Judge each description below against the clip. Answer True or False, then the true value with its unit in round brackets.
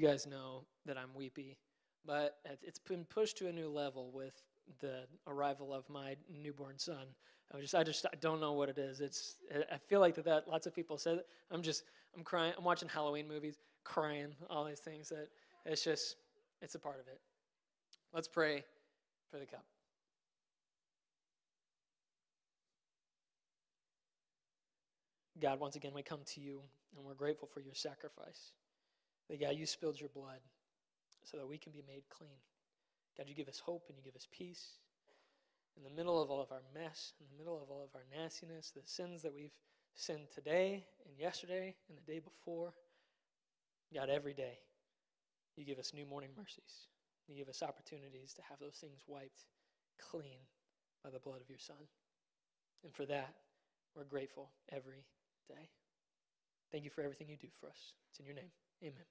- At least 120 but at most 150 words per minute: False (175 wpm)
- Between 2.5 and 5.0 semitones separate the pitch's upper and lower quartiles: True (2.9 semitones)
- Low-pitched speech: False (150 Hz)